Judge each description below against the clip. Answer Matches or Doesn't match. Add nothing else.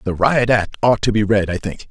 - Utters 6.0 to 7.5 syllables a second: Doesn't match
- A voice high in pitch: Doesn't match